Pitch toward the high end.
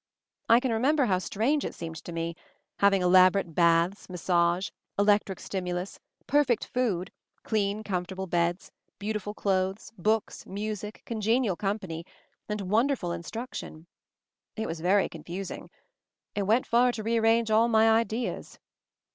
Yes: high, 200 Hz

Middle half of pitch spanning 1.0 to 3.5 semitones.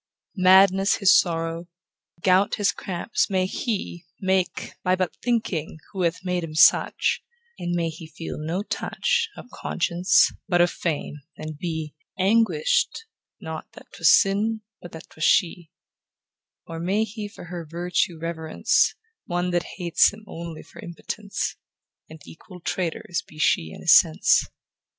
Yes: average, 2.9 semitones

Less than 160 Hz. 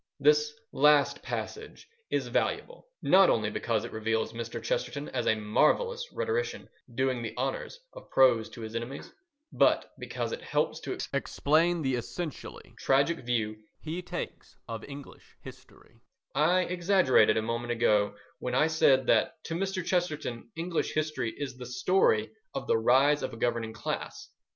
Yes: medium, 140 Hz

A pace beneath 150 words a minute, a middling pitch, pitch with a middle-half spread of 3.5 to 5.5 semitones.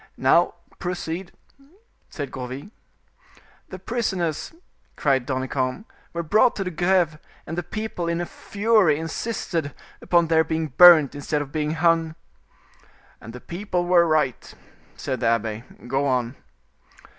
Yes: slow, 135 wpm; medium, 160 Hz; average, 4.2 semitones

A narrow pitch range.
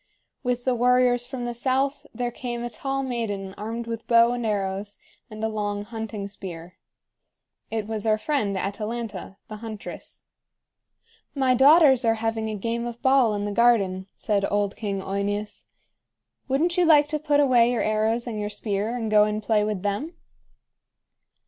No: average, 3.1 semitones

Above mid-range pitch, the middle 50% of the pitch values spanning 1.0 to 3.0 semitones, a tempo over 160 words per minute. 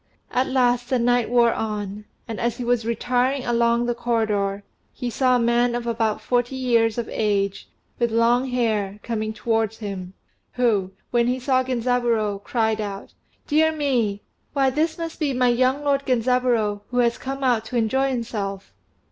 Yes: high, 240 Hz; narrow, 2.5 semitones; average, 170 wpm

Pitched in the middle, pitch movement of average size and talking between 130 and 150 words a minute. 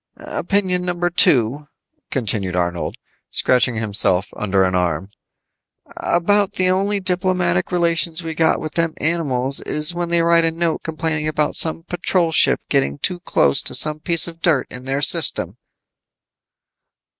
No: medium, 160 Hz; wide, 5.7 semitones; average, 145 wpm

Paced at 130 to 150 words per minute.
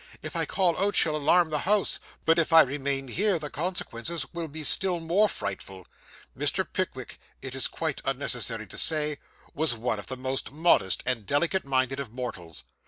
No: average, 180 wpm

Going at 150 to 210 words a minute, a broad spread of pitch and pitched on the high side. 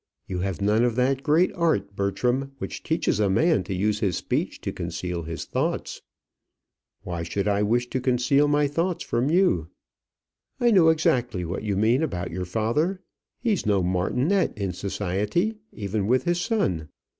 No: average, 170 wpm; wide, 7.7 semitones; low, 110 Hz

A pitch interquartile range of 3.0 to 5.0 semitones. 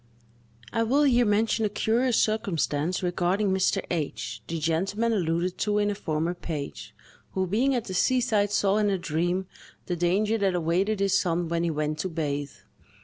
Yes: average, 4.1 semitones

